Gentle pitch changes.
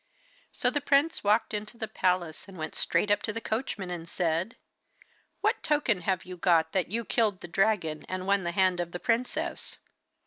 No: average, 4.0 semitones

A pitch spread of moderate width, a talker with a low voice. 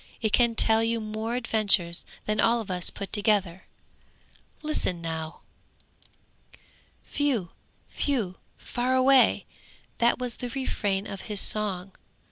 No: average, 3.8 semitones; high, 215 Hz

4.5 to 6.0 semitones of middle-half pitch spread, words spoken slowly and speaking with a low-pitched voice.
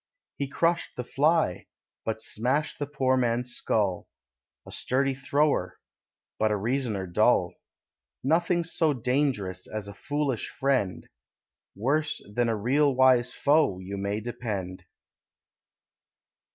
Yes: average, 5.3 semitones; slow, 120 wpm; low, 125 Hz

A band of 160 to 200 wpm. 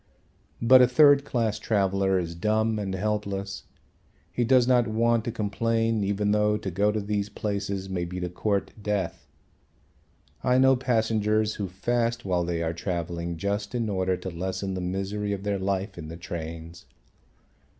Yes: average, 165 wpm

